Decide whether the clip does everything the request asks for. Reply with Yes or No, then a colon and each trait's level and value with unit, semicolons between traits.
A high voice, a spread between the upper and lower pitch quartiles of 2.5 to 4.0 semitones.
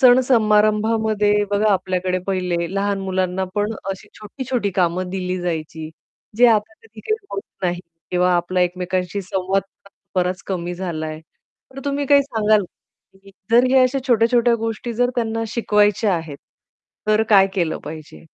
Yes: high, 205 Hz; average, 3.7 semitones